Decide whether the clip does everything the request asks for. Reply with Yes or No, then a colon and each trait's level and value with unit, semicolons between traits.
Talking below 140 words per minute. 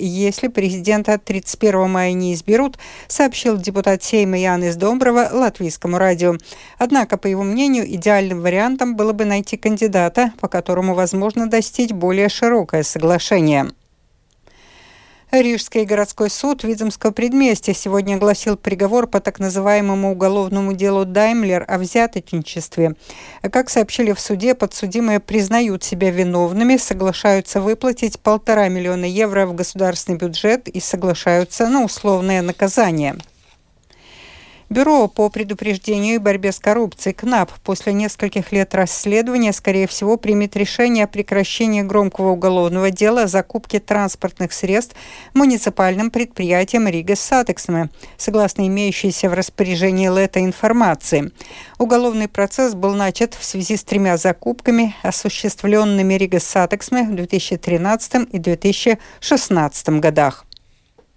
Yes: average, 120 wpm